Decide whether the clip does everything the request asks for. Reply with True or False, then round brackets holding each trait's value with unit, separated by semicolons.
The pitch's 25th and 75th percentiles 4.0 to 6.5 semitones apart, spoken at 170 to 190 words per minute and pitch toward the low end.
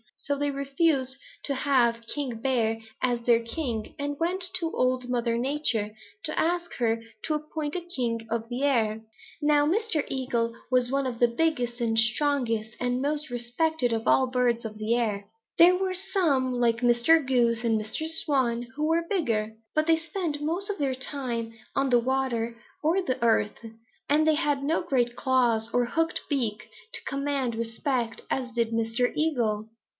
False (4.3 semitones; 175 wpm; 255 Hz)